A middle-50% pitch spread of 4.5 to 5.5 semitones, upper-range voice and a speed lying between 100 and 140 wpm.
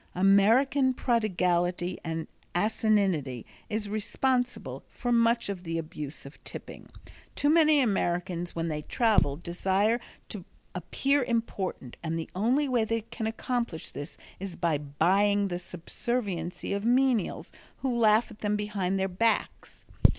Yes: average, 5.0 semitones; high, 200 Hz; slow, 135 wpm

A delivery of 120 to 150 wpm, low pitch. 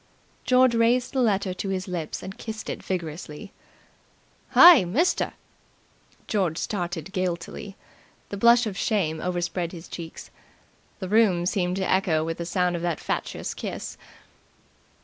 No: average, 140 wpm; medium, 185 Hz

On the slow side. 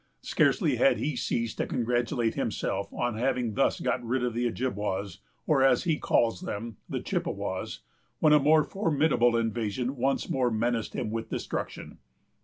No: average, 160 wpm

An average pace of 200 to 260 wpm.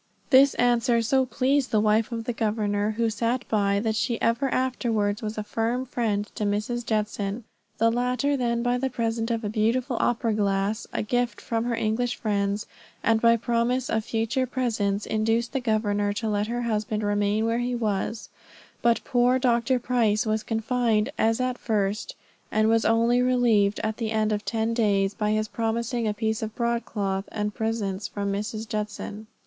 No: average, 180 wpm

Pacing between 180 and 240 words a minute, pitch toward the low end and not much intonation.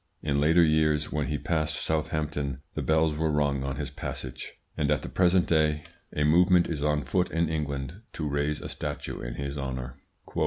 Yes: average, 190 wpm; very low, 75 Hz; narrow, 1.9 semitones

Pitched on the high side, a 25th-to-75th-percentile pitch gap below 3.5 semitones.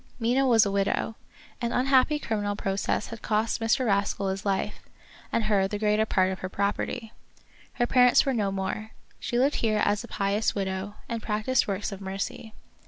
Yes: high, 210 Hz; average, 2.8 semitones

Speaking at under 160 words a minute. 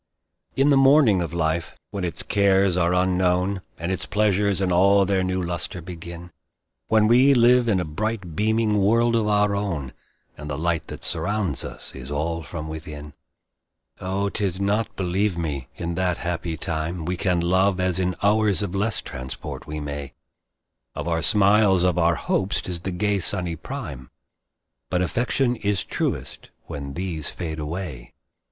No: average, 165 wpm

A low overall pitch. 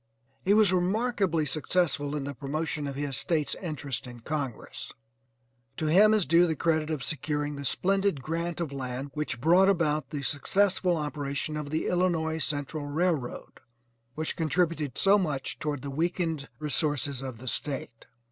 No: medium, 155 Hz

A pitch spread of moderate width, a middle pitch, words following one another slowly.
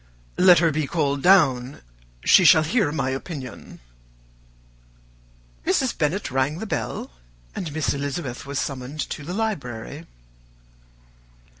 Yes: average, 4.4 semitones; medium, 150 Hz; slow, 120 wpm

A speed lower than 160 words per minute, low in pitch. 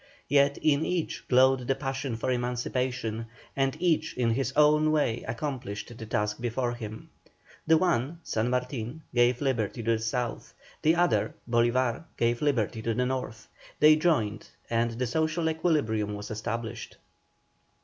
Yes: average, 150 wpm; low, 125 Hz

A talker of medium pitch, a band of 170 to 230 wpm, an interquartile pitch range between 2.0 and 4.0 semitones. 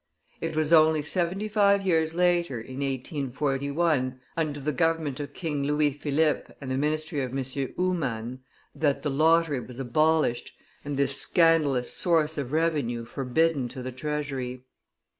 No: medium, 150 Hz; average, 145 wpm; average, 3.4 semitones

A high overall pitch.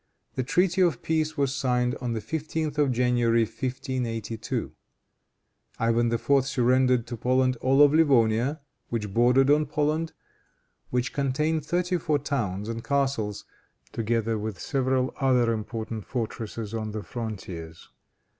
No: low, 125 Hz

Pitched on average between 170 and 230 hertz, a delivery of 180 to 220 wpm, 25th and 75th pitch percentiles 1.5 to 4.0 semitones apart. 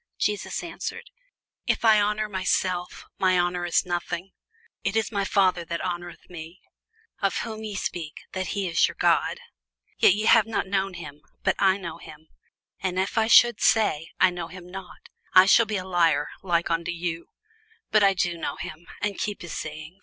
Yes: medium, 185 Hz; average, 185 wpm; average, 2.8 semitones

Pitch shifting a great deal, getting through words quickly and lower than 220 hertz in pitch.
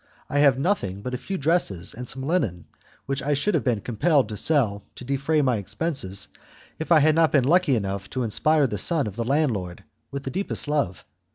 Yes: wide, 6.4 semitones; fast, 210 wpm; low, 135 Hz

